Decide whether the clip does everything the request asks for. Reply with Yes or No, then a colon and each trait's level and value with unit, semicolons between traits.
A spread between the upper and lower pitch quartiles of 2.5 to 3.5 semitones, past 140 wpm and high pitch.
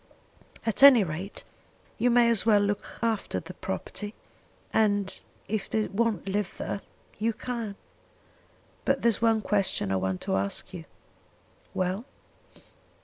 No: average, 3.2 semitones; slow, 135 wpm; high, 205 Hz